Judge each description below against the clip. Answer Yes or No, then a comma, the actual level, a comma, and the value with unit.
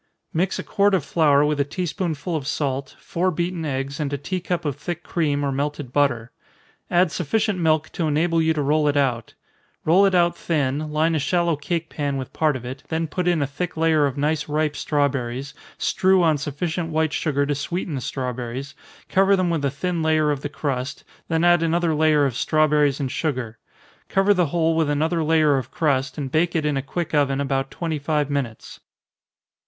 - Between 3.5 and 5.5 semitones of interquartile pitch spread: No, average, 3.0 semitones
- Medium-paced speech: No, fast, 210 wpm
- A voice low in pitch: No, medium, 150 Hz